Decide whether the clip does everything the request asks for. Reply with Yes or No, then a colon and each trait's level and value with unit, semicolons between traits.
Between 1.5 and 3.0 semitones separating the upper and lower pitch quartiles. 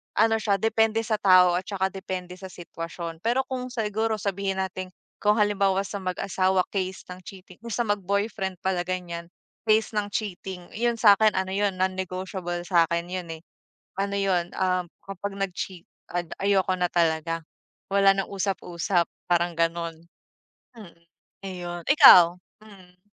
Yes: narrow, 2.4 semitones